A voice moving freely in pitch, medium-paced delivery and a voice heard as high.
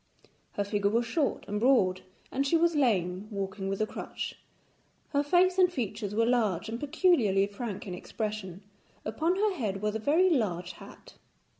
Yes: wide, 6.4 semitones; average, 170 wpm; high, 220 Hz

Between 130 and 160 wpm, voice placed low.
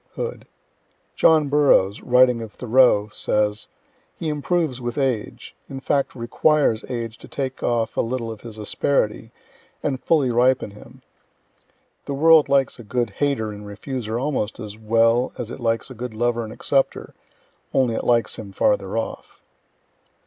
Yes: average, 155 wpm; low, 120 Hz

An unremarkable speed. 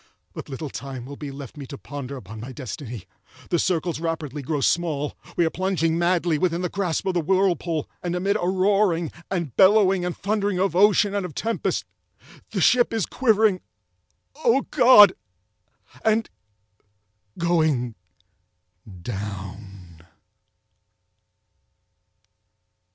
No: slow, 120 wpm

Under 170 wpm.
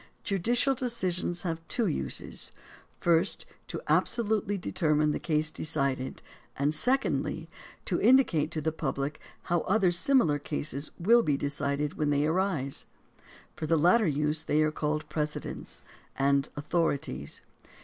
Yes: average, 140 wpm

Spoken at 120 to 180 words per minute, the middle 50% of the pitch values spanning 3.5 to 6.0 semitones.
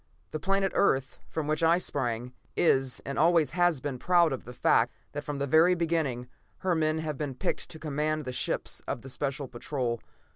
No: average, 195 wpm; average, 3.8 semitones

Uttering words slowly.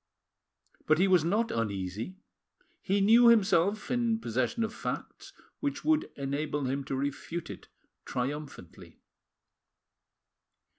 Yes: slow, 110 wpm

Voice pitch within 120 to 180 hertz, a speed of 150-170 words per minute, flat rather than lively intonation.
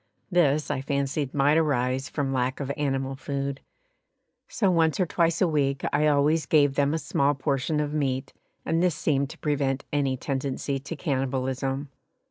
Yes: medium, 140 Hz; average, 165 wpm; narrow, 2.1 semitones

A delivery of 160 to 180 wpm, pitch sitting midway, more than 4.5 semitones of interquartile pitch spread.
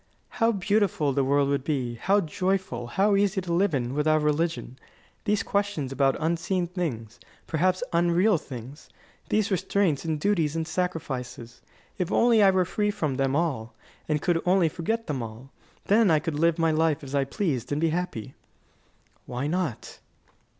Yes: average, 170 wpm; medium, 165 Hz; average, 5.2 semitones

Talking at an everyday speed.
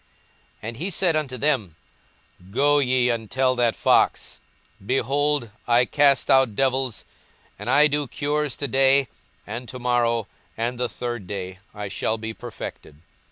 Yes: average, 155 wpm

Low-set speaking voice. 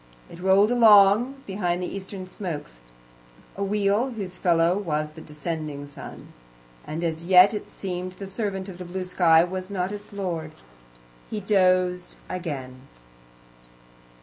No: medium, 185 Hz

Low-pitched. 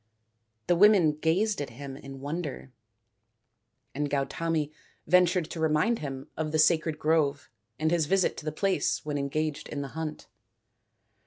No: medium, 155 Hz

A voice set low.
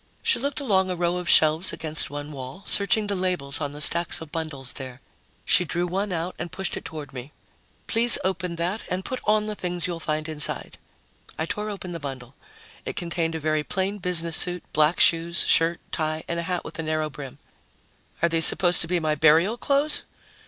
No: medium, 170 Hz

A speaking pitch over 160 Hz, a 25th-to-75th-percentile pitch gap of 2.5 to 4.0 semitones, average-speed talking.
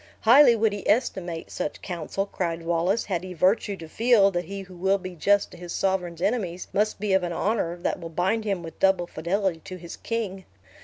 No: high, 190 Hz; average, 2.8 semitones; fast, 210 wpm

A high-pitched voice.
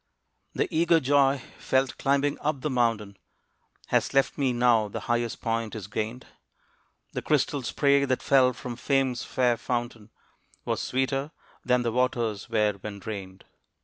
No: low, 125 Hz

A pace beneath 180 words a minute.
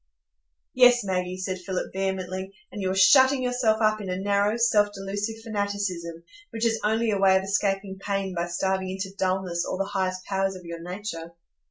No: average, 185 wpm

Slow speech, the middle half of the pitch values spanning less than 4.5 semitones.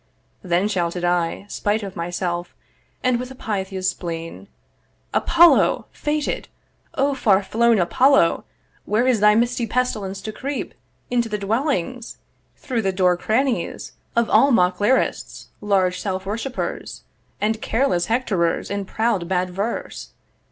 No: slow, 130 wpm; average, 4.9 semitones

